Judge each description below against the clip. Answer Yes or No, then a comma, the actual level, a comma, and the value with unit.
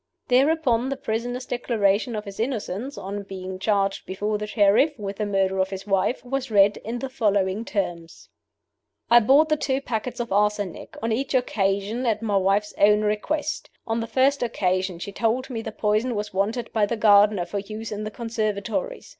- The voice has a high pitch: Yes, high, 215 Hz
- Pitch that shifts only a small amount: No, average, 3.4 semitones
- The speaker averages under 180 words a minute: No, average, 190 wpm